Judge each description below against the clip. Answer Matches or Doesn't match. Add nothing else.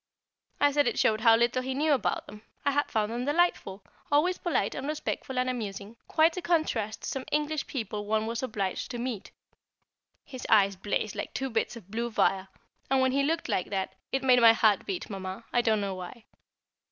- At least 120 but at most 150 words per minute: Doesn't match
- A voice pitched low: Doesn't match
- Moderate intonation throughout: Matches